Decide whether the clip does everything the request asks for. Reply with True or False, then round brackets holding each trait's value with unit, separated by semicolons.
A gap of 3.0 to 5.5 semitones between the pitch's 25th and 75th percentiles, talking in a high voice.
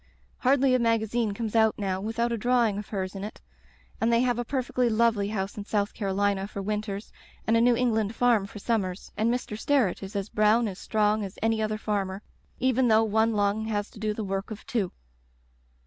False (2.4 semitones; 215 Hz)